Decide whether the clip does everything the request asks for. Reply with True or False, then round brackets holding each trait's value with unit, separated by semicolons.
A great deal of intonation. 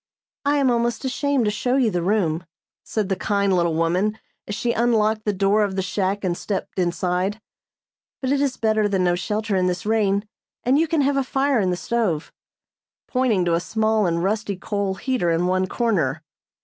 False (4.2 semitones)